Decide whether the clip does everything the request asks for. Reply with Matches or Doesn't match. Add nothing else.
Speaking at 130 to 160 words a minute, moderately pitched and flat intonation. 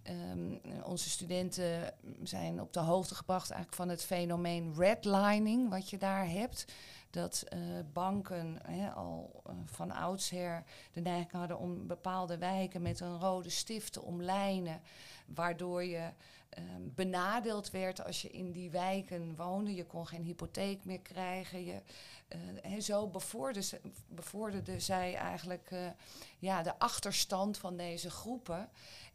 Matches